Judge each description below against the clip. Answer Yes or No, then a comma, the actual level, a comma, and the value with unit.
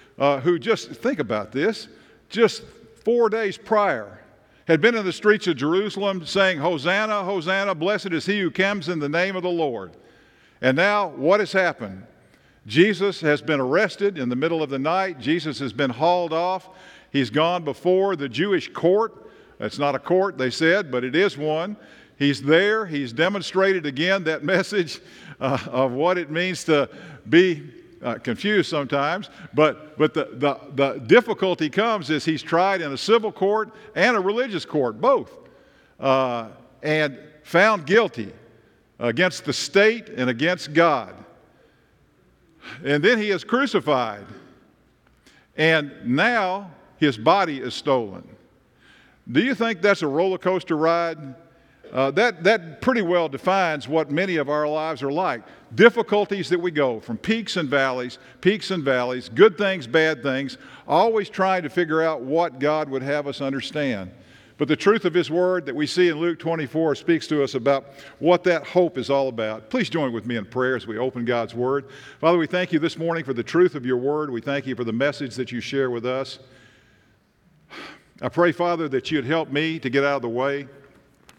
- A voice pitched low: No, medium, 160 Hz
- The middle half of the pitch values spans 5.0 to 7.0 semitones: Yes, average, 5.3 semitones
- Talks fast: No, average, 175 wpm